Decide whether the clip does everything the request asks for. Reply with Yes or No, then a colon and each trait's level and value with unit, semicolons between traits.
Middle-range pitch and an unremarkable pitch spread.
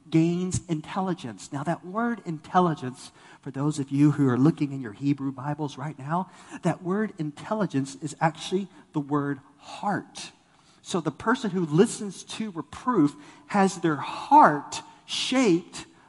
Yes: medium, 160 Hz; average, 5.0 semitones